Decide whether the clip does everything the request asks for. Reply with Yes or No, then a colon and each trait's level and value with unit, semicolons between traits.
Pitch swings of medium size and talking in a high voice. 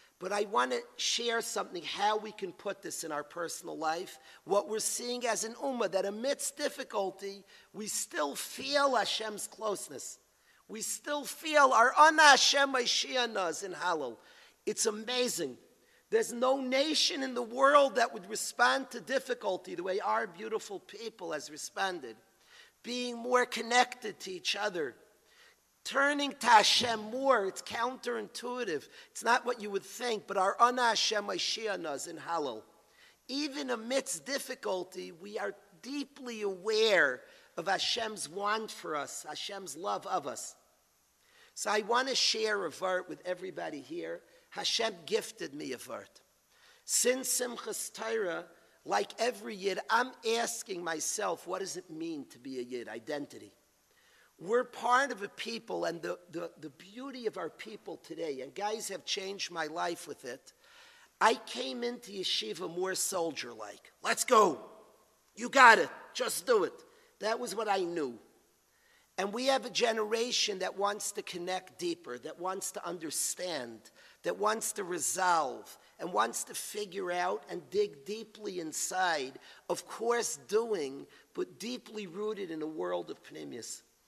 No: wide, 6.0 semitones; high, 235 Hz